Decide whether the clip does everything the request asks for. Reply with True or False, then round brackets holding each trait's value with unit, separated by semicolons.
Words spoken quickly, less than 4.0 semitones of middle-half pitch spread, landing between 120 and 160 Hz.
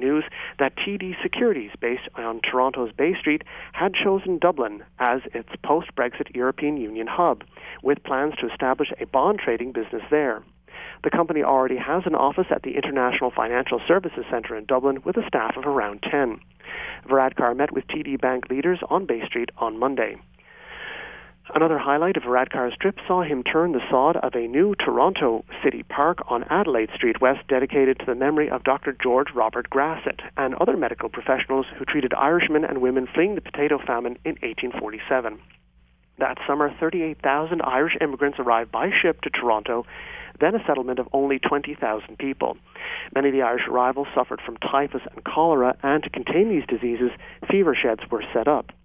False (170 wpm; 3.3 semitones; 135 Hz)